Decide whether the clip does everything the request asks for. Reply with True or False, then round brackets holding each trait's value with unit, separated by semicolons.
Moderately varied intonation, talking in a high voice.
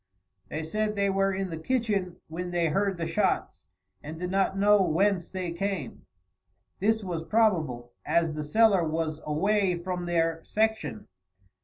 False (3.7 semitones; 180 Hz)